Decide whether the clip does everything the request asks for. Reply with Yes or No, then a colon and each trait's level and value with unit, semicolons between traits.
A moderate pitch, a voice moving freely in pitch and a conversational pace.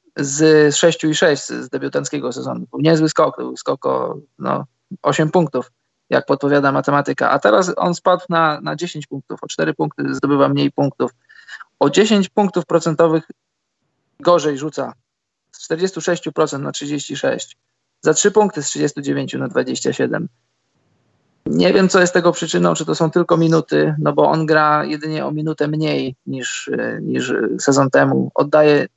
Yes: medium, 150 Hz; wide, 7.6 semitones; average, 150 wpm